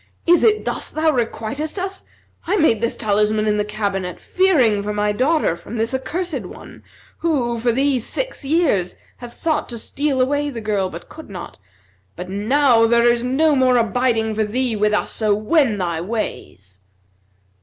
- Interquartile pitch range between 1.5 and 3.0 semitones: No, wide, 5.6 semitones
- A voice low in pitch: No, high, 235 Hz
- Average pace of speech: Yes, average, 175 wpm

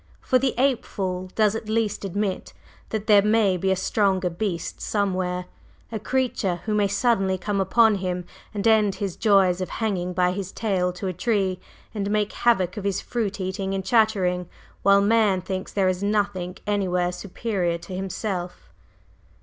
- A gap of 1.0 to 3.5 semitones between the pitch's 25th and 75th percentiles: Yes, narrow, 2.6 semitones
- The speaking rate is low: No, average, 170 wpm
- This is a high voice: Yes, high, 195 Hz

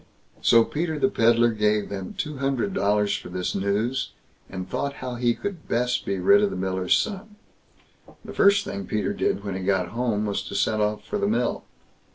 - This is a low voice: Yes, low, 115 Hz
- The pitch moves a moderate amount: No, wide, 7.0 semitones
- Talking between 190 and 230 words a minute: Yes, average, 200 wpm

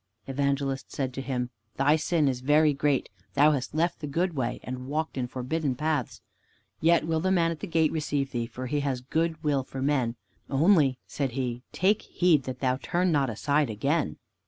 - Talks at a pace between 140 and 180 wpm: No, average, 195 wpm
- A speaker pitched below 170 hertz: Yes, medium, 140 Hz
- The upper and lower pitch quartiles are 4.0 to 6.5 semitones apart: No, average, 3.5 semitones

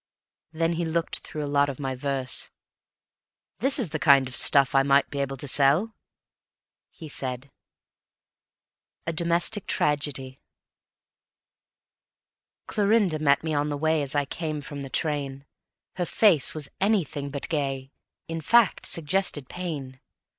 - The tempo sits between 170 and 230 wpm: No, average, 140 wpm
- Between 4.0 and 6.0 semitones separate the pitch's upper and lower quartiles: No, average, 3.3 semitones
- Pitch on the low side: No, medium, 145 Hz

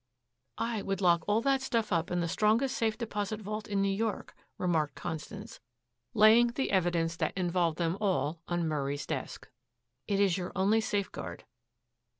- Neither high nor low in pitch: No, high, 195 Hz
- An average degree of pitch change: Yes, average, 4.2 semitones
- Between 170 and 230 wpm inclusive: No, average, 160 wpm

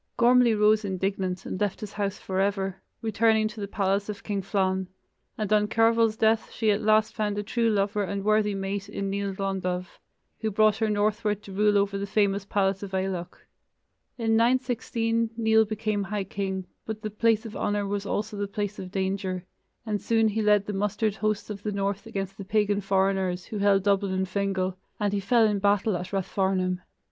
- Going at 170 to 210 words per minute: Yes, average, 190 wpm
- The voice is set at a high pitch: Yes, high, 205 Hz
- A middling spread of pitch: No, narrow, 1.8 semitones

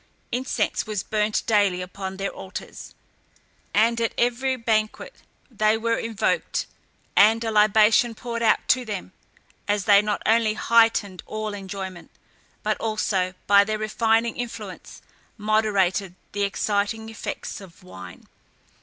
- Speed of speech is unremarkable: No, slow, 130 wpm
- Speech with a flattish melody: Yes, narrow, 2.2 semitones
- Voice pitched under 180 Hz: No, high, 215 Hz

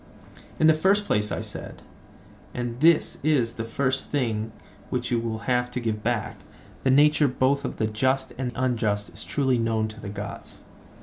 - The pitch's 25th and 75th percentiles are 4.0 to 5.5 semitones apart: No, average, 3.5 semitones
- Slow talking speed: No, average, 170 wpm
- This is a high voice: No, low, 125 Hz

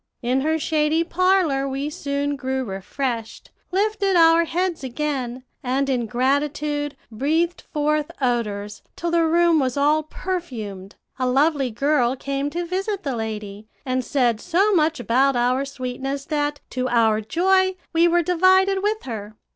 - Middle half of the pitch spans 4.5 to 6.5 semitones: Yes, average, 5.0 semitones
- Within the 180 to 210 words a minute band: No, average, 145 wpm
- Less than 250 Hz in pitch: No, very high, 285 Hz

